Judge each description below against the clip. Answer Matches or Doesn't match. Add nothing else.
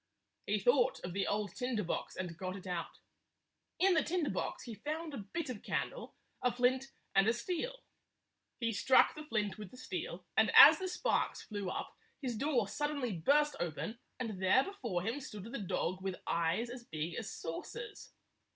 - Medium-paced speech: Matches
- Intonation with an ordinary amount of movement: Doesn't match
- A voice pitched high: Matches